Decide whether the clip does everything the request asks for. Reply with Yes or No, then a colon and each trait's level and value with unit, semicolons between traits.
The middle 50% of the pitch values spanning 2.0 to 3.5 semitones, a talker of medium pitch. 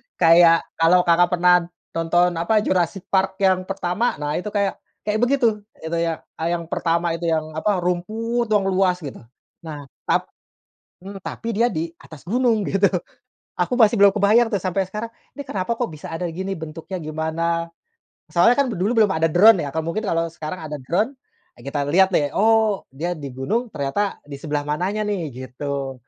No: average, 4.4 semitones; medium, 180 Hz